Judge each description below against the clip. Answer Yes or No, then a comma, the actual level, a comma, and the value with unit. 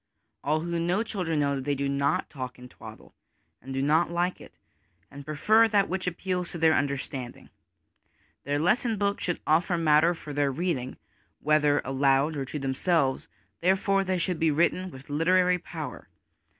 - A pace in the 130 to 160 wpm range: No, average, 170 wpm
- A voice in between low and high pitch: Yes, medium, 160 Hz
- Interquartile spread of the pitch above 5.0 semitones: No, average, 4.4 semitones